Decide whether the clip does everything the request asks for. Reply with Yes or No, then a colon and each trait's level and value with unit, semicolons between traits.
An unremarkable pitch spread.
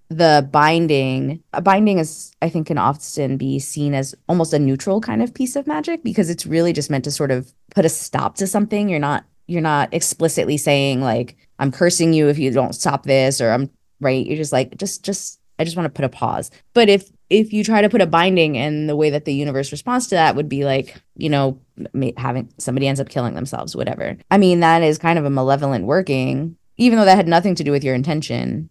Yes: average, 4.3 semitones